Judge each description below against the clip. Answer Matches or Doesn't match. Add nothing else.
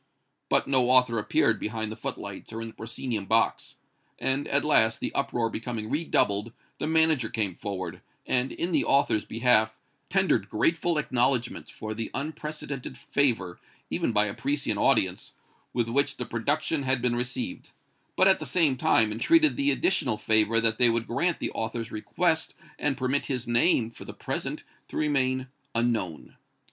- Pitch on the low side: Matches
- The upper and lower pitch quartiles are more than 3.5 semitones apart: Matches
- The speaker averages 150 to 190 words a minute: Matches